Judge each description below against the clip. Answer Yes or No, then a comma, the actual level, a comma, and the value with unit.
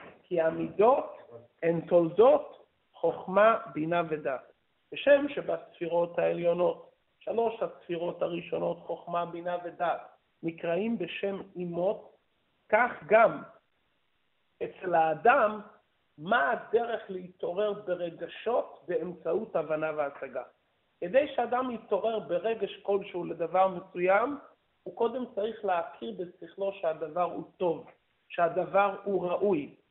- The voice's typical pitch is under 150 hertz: No, medium, 180 Hz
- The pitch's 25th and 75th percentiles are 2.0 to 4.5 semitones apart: Yes, average, 3.6 semitones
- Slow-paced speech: Yes, slow, 95 wpm